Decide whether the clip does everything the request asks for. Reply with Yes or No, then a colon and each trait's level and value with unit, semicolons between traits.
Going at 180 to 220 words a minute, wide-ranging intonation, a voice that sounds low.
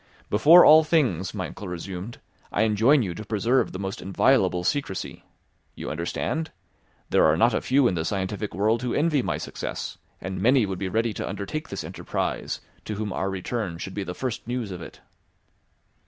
No: average, 185 wpm; average, 4.9 semitones; low, 105 Hz